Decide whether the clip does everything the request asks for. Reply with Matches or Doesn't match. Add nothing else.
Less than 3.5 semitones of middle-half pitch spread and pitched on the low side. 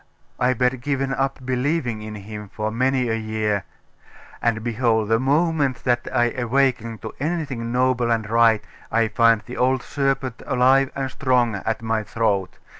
Matches